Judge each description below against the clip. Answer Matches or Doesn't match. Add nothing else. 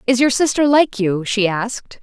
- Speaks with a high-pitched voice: Matches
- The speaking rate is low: Doesn't match